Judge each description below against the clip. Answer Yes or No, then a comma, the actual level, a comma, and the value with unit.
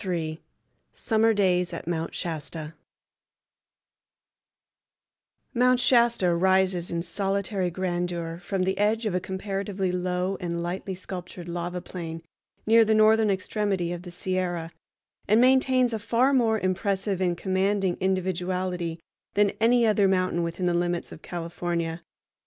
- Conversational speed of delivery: No, slow, 130 wpm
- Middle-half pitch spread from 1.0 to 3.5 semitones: Yes, average, 2.8 semitones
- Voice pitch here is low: No, medium, 185 Hz